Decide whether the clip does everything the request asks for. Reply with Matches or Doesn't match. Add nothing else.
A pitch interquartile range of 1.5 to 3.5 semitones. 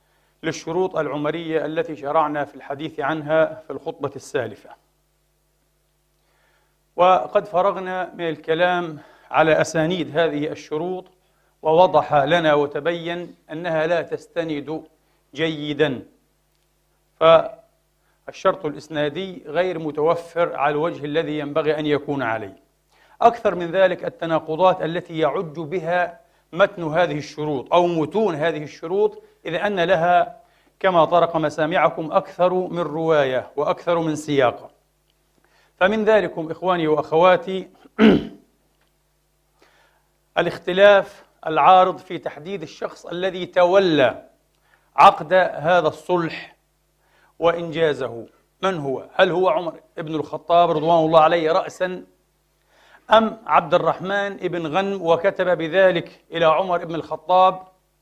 Matches